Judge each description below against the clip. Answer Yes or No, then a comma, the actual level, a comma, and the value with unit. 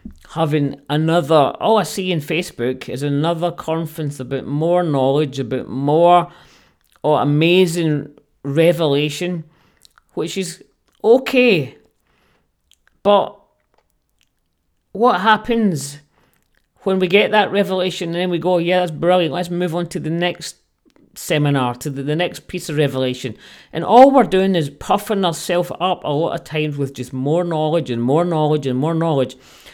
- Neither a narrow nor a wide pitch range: Yes, average, 3.6 semitones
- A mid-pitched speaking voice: Yes, medium, 165 Hz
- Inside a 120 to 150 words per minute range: Yes, average, 145 wpm